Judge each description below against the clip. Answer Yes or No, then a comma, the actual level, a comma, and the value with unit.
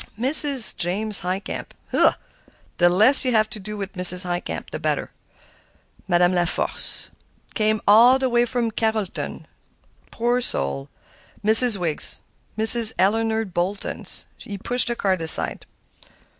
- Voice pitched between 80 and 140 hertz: No, high, 215 Hz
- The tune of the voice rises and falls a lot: No, average, 4.2 semitones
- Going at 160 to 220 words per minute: No, slow, 135 wpm